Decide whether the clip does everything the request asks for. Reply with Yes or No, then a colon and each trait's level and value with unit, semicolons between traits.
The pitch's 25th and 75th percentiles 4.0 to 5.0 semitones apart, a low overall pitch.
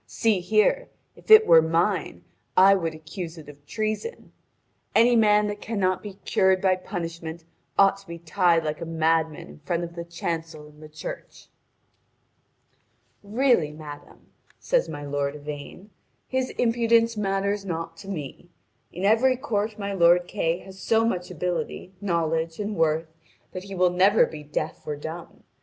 No: average, 4.3 semitones; medium, 180 Hz